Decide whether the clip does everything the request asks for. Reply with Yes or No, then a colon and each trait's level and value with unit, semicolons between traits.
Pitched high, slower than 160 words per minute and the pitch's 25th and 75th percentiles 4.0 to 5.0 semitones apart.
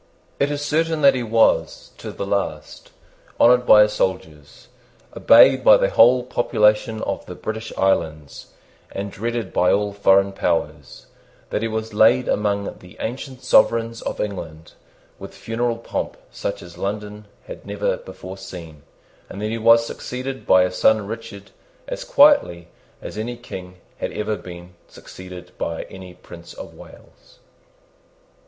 No: low, 105 Hz; average, 150 wpm; average, 4.3 semitones